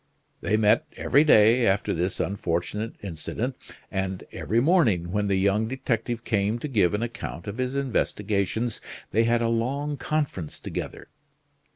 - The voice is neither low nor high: No, low, 110 Hz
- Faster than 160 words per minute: No, average, 150 wpm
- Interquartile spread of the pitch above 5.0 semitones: No, average, 3.8 semitones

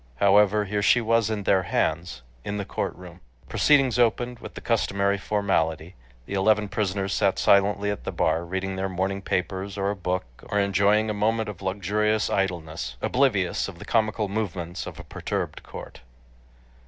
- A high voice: No, low, 100 Hz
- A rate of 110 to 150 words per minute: No, average, 165 wpm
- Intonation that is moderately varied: No, narrow, 2.3 semitones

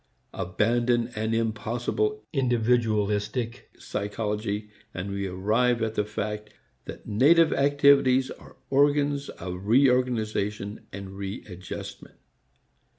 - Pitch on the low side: Yes, low, 110 Hz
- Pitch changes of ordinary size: Yes, average, 3.6 semitones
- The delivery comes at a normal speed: No, slow, 100 wpm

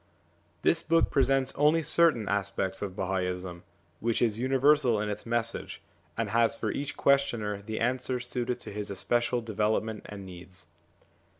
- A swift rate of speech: No, average, 155 wpm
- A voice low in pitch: Yes, low, 115 Hz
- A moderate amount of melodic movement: Yes, average, 4.1 semitones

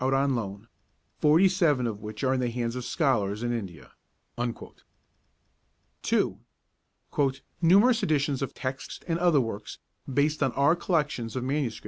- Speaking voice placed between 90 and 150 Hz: Yes, low, 135 Hz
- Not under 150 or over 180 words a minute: No, average, 140 wpm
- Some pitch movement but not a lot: Yes, average, 4.7 semitones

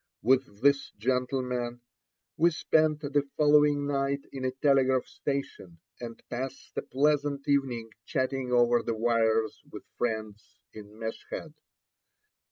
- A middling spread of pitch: Yes, average, 3.2 semitones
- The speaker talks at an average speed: No, slow, 120 wpm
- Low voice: Yes, low, 130 Hz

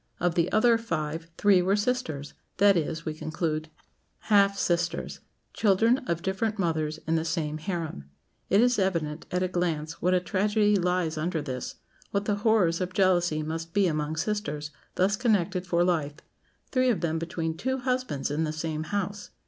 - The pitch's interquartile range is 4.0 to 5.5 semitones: Yes, average, 4.3 semitones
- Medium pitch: Yes, medium, 175 Hz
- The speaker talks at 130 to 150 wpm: No, average, 170 wpm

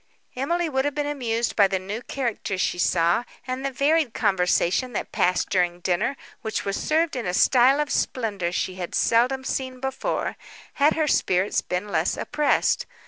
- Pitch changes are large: Yes, wide, 6.6 semitones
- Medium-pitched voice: No, high, 240 Hz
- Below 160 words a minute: No, average, 175 wpm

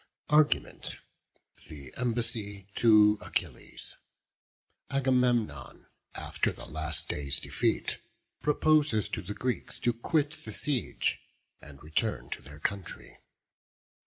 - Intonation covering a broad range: Yes, wide, 8.7 semitones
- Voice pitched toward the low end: Yes, low, 110 Hz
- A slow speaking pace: Yes, slow, 100 wpm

